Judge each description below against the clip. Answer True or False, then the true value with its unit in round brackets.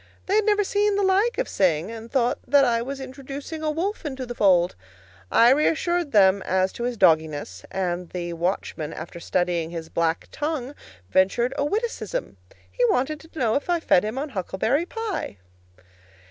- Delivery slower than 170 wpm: False (175 wpm)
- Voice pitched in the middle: False (250 Hz)